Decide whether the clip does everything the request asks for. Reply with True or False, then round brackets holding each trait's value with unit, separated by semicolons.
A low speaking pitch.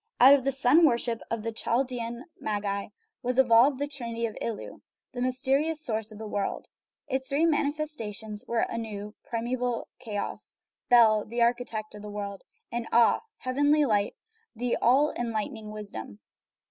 False (235 Hz)